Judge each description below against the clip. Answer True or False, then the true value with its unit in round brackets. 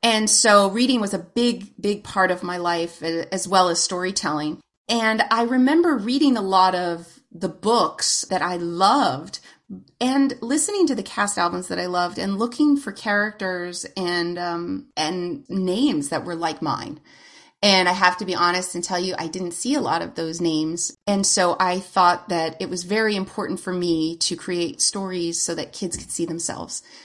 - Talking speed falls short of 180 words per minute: False (190 wpm)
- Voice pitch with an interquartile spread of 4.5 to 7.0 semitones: False (4.1 semitones)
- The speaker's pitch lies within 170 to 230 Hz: True (185 Hz)